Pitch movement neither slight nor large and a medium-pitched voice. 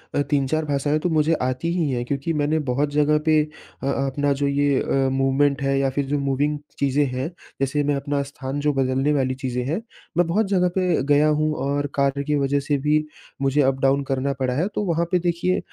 No: narrow, 2.0 semitones; medium, 145 Hz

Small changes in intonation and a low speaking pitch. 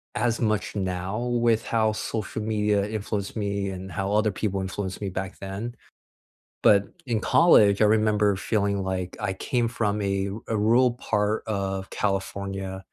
Yes: narrow, 2.1 semitones; low, 105 Hz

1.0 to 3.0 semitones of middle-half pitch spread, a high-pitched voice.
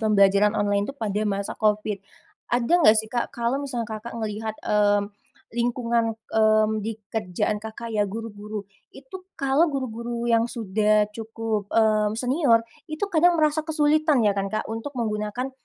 Yes: narrow, 2.5 semitones; high, 225 Hz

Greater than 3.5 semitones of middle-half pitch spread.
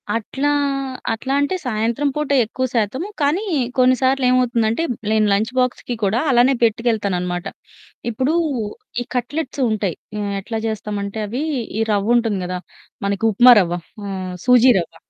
Yes: average, 4.0 semitones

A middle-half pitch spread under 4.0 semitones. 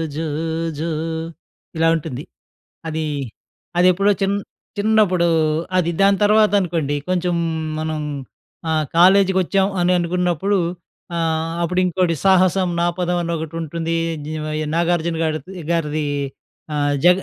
Yes: narrow, 2.4 semitones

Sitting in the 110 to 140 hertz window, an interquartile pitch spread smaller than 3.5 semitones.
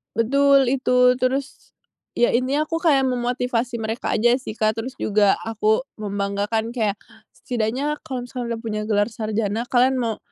No: high, 235 Hz; average, 2.8 semitones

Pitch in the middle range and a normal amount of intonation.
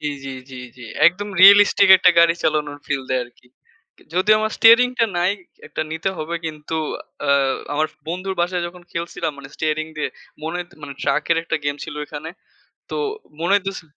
Yes: medium, 170 Hz; average, 3.8 semitones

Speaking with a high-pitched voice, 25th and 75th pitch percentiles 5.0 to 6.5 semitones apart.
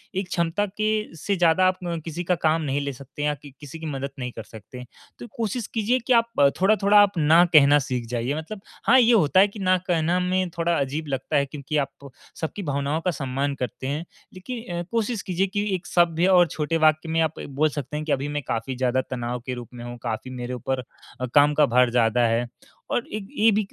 No: medium, 155 Hz; wide, 5.5 semitones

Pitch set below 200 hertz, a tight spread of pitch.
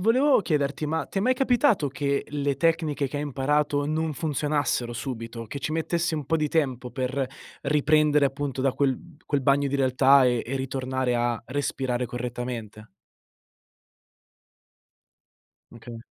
No: medium, 140 Hz; average, 3.0 semitones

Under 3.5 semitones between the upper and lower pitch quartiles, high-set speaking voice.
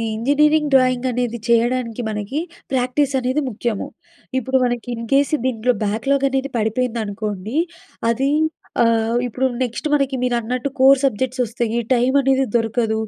Yes: average, 2.7 semitones; very high, 250 Hz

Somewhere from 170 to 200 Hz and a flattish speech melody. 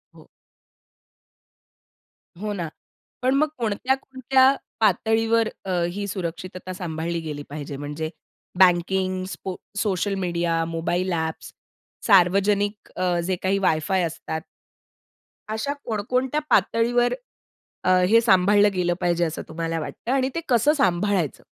No: high, 190 Hz; average, 4.6 semitones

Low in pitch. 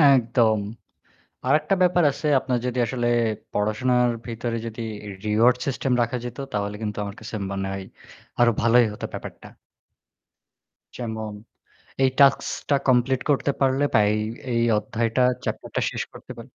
Yes: low, 120 Hz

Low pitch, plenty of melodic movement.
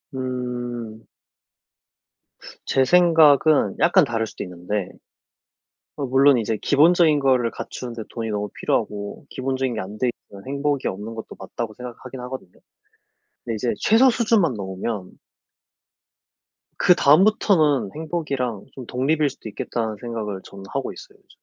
No: low, 125 Hz; average, 4.9 semitones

